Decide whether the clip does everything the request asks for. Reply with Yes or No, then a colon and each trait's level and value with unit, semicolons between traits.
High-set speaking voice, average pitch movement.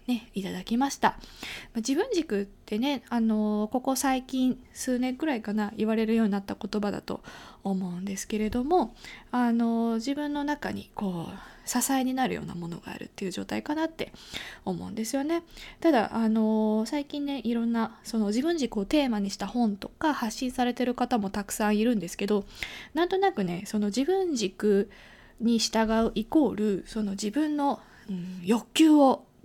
Yes: high, 230 Hz; average, 4.2 semitones